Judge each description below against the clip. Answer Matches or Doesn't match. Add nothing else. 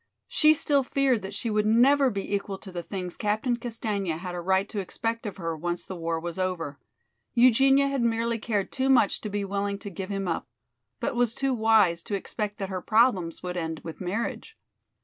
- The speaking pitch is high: Matches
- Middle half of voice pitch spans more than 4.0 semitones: Matches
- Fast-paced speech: Matches